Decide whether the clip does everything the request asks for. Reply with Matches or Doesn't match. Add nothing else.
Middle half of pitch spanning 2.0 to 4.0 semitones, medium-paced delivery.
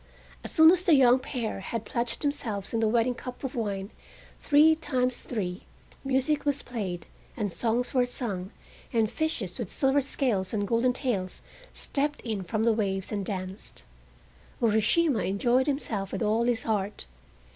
Doesn't match